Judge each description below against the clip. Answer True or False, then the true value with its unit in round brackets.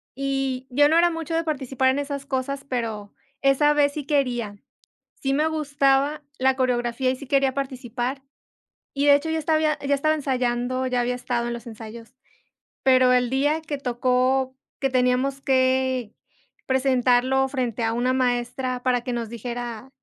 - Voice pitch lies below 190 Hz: False (260 Hz)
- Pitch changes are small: True (2.1 semitones)